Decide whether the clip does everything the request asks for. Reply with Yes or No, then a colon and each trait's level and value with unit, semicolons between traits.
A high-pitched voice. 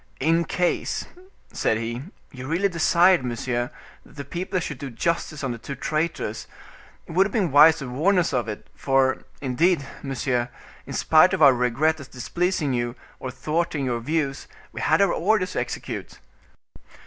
No: medium, 145 Hz